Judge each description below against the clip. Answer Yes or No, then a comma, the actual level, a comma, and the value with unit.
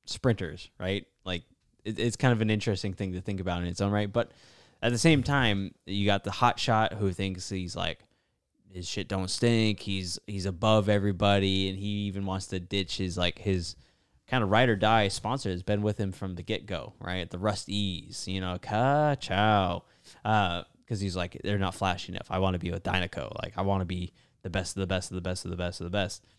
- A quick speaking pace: Yes, fast, 230 wpm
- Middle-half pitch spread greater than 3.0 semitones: No, narrow, 2.6 semitones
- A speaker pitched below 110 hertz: Yes, low, 100 Hz